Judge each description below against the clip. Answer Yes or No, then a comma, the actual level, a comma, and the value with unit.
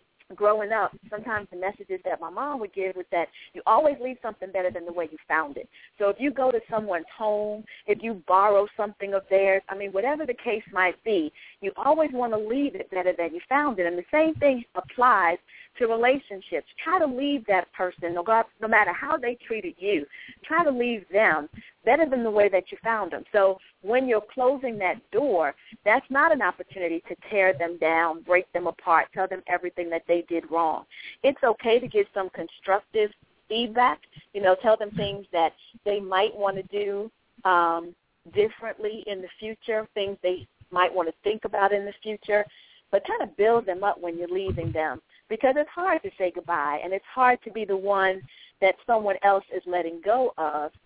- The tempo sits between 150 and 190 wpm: No, average, 200 wpm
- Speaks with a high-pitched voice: Yes, high, 200 Hz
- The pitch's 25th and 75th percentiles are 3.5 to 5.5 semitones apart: Yes, average, 4.2 semitones